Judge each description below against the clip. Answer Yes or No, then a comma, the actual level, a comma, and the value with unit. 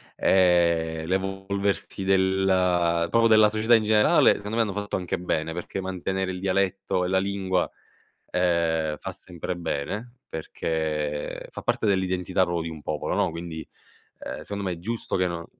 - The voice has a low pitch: Yes, very low, 95 Hz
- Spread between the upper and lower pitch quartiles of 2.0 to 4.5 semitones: Yes, narrow, 2.6 semitones